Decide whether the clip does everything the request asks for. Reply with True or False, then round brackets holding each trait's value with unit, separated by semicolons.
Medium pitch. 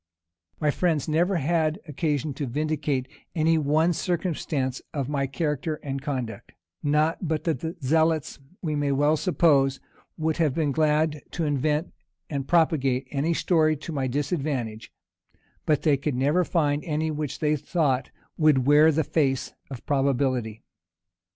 True (150 Hz)